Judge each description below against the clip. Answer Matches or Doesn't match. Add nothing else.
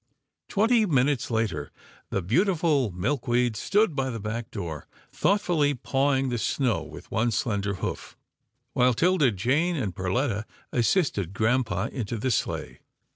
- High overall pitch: Doesn't match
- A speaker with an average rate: Doesn't match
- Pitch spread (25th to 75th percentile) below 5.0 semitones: Doesn't match